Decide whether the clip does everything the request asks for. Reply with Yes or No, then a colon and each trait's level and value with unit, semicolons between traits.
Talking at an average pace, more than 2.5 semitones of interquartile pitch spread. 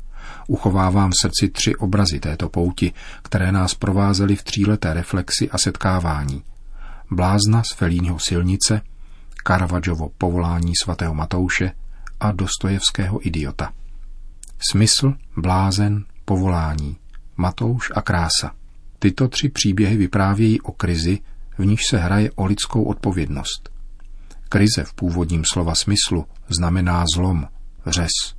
No: slow, 110 wpm; average, 2.9 semitones